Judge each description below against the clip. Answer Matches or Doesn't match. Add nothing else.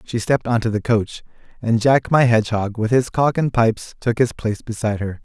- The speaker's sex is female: Doesn't match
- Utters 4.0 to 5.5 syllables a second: Doesn't match